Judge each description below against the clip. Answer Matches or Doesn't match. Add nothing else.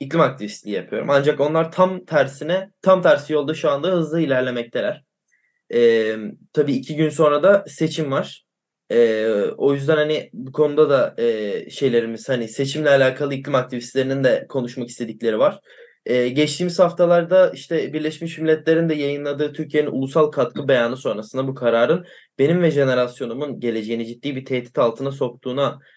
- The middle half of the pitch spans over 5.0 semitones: Doesn't match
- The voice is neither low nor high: Matches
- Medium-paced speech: Doesn't match